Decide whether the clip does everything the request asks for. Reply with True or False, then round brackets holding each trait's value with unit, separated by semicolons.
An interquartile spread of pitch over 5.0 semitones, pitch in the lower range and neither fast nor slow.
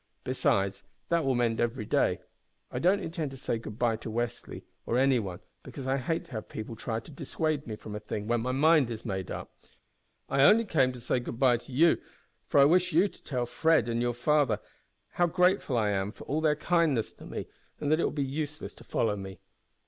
False (5.4 semitones; 130 Hz; 225 wpm)